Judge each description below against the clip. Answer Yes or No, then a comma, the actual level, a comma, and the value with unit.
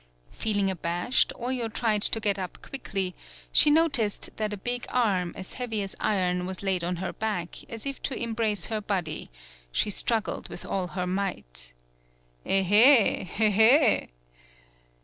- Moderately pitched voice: No, high, 205 Hz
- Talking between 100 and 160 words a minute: Yes, average, 150 wpm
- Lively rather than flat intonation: No, average, 3.7 semitones